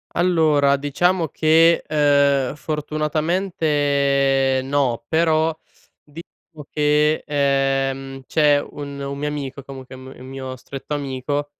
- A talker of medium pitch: Yes, medium, 145 Hz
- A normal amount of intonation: No, narrow, 2.2 semitones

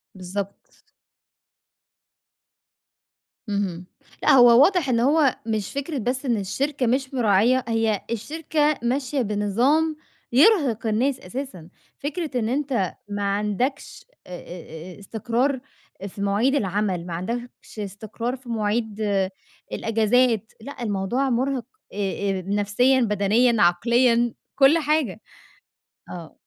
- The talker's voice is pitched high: Yes, high, 235 Hz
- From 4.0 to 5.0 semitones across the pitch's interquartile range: Yes, average, 4.7 semitones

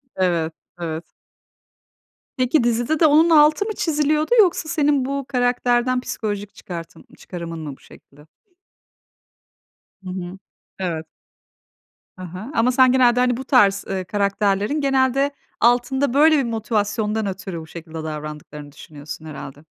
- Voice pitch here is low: No, high, 220 Hz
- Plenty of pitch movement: Yes, wide, 7.7 semitones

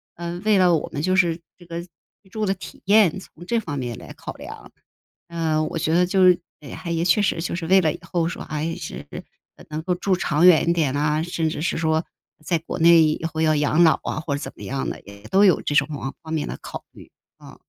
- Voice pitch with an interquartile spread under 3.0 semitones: Yes, narrow, 2.5 semitones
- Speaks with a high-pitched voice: No, medium, 165 Hz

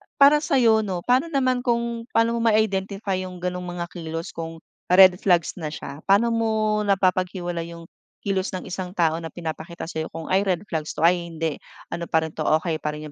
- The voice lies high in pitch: No, medium, 180 Hz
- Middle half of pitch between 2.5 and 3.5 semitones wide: No, average, 4.7 semitones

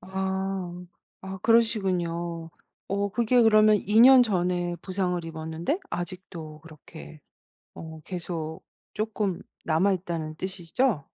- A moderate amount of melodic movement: Yes, average, 3.3 semitones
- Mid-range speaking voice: Yes, medium, 180 Hz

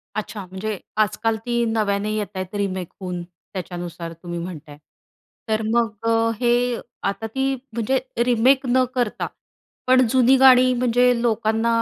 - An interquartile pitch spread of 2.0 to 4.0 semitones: No, average, 4.6 semitones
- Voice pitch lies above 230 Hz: No, high, 220 Hz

